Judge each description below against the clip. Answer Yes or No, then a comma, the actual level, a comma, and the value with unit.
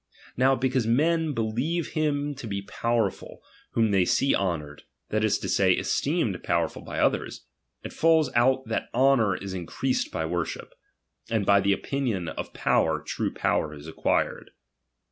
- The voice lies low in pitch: Yes, low, 115 Hz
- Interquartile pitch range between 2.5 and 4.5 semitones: No, wide, 5.6 semitones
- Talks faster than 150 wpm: Yes, average, 160 wpm